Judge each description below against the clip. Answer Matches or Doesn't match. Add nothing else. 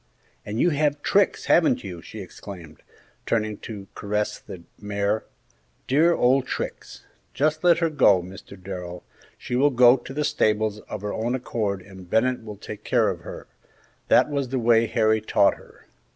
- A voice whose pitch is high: Doesn't match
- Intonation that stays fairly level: Doesn't match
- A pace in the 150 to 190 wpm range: Matches